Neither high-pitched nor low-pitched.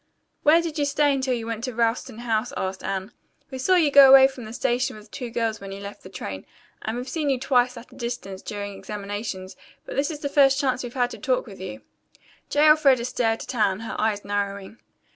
No: high, 240 Hz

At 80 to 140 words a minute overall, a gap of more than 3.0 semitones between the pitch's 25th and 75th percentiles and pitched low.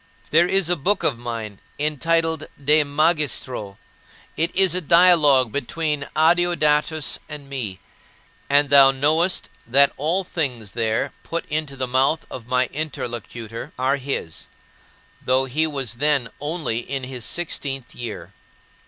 No: slow, 135 wpm; average, 3.8 semitones; medium, 145 Hz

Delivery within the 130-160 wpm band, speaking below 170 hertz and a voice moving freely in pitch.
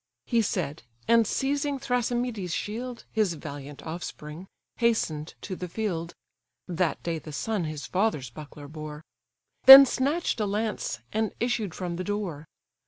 No: average, 140 wpm; high, 190 Hz; wide, 6.8 semitones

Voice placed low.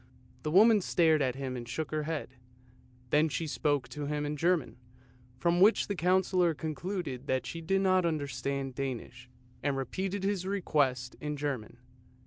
No: medium, 150 Hz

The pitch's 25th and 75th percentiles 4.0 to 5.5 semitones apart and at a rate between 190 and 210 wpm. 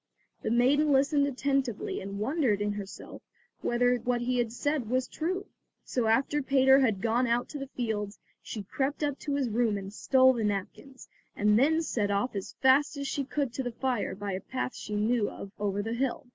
Yes: average, 4.5 semitones; average, 200 wpm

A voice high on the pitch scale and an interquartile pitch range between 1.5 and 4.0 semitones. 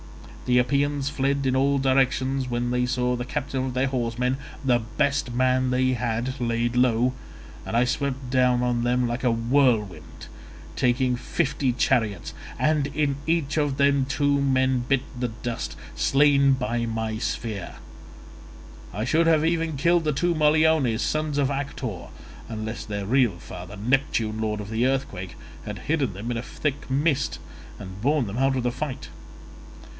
No: low, 130 Hz; average, 2.8 semitones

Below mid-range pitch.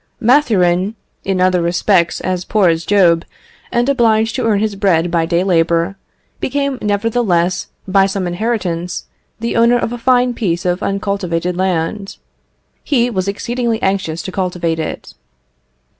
No: high, 195 Hz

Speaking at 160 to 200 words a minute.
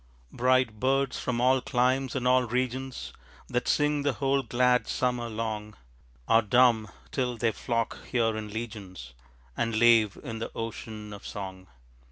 No: average, 150 wpm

